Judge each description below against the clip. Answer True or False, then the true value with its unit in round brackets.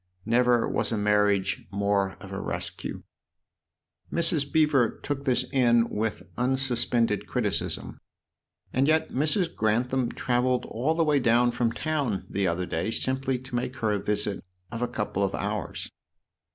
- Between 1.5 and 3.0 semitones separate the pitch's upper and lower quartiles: False (4.1 semitones)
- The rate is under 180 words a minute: True (150 wpm)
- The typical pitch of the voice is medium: False (120 Hz)